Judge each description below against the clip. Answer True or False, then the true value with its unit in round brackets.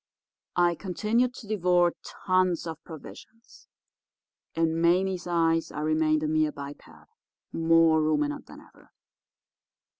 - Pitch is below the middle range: False (165 Hz)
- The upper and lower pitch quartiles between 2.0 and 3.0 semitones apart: True (2.6 semitones)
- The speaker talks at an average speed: False (115 wpm)